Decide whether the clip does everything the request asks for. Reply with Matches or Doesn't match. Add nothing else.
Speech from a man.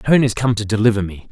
Matches